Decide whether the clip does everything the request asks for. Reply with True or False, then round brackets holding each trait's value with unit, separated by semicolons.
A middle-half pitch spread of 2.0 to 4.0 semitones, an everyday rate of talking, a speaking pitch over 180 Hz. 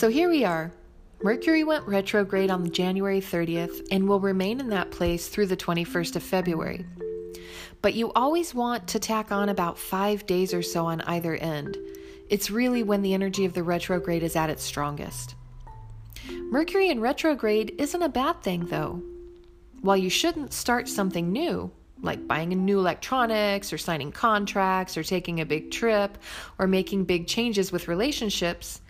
False (4.5 semitones; 165 wpm; 190 Hz)